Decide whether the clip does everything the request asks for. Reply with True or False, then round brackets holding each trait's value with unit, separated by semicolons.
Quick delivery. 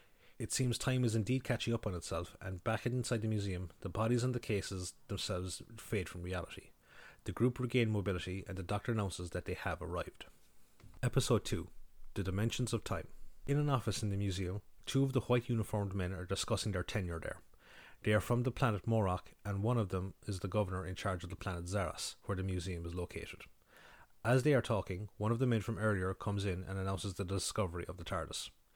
True (210 wpm)